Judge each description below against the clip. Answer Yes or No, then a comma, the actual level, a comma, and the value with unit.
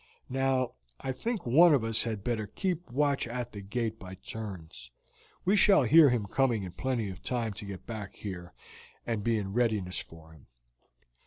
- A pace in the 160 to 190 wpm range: Yes, average, 180 wpm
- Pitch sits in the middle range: No, low, 115 Hz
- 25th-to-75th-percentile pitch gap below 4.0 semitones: No, average, 4.8 semitones